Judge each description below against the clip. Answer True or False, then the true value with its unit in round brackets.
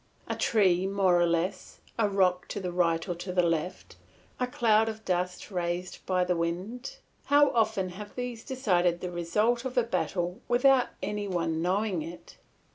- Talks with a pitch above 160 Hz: True (185 Hz)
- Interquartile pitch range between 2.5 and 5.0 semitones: True (4.1 semitones)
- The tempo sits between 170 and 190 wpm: True (175 wpm)